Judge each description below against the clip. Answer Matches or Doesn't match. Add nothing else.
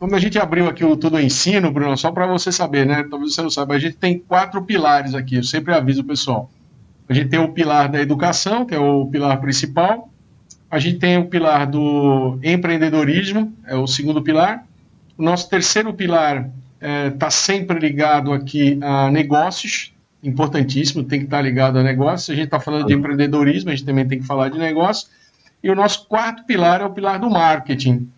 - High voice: Doesn't match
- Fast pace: Matches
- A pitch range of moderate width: Matches